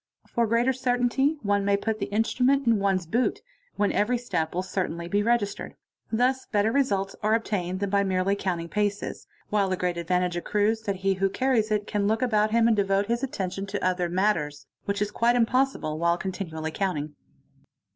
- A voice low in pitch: No, high, 205 Hz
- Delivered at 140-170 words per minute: No, average, 185 wpm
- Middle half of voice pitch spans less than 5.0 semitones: Yes, average, 3.7 semitones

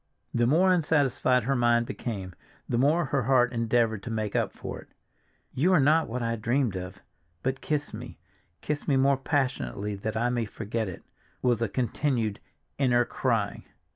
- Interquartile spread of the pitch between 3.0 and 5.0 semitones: Yes, average, 3.6 semitones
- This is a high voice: No, low, 120 Hz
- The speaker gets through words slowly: No, average, 165 wpm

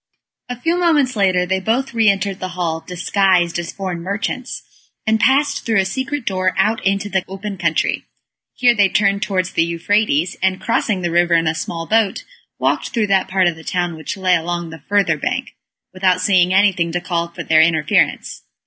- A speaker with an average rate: Yes, average, 195 wpm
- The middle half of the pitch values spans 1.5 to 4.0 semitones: Yes, average, 3.5 semitones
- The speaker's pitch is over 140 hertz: Yes, high, 190 Hz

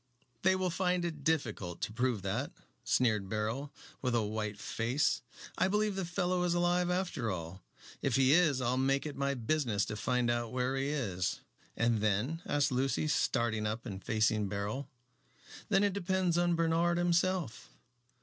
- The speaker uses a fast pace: No, average, 170 wpm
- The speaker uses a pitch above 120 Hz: Yes, low, 135 Hz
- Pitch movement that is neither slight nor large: No, wide, 7.8 semitones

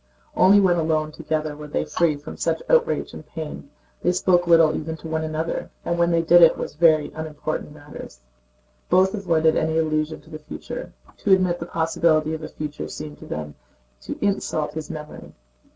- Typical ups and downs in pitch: No, narrow, 1.9 semitones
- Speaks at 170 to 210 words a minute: Yes, average, 190 wpm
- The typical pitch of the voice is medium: Yes, medium, 160 Hz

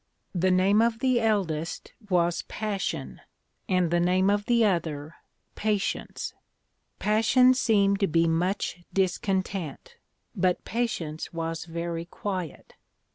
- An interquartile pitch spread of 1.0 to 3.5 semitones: No, average, 3.9 semitones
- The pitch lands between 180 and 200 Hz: Yes, medium, 185 Hz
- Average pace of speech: No, slow, 115 wpm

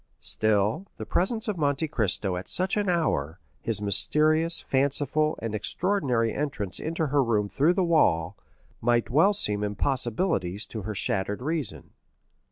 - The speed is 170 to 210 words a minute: No, average, 145 wpm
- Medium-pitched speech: No, low, 130 Hz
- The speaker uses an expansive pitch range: Yes, wide, 7.5 semitones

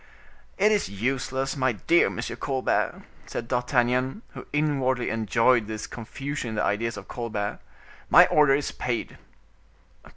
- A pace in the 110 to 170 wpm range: Yes, slow, 135 wpm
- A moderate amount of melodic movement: Yes, average, 3.2 semitones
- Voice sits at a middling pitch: No, low, 125 Hz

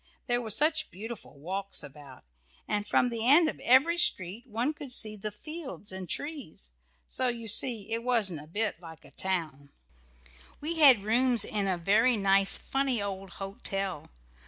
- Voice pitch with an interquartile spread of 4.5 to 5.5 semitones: Yes, average, 4.9 semitones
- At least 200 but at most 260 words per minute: No, average, 170 wpm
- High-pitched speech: Yes, high, 215 Hz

